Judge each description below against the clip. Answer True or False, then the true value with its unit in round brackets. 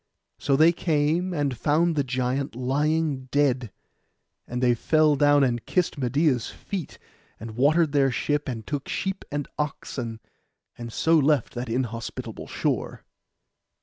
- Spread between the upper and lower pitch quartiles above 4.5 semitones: False (3.6 semitones)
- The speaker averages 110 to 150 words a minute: True (140 wpm)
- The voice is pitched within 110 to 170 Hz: True (140 Hz)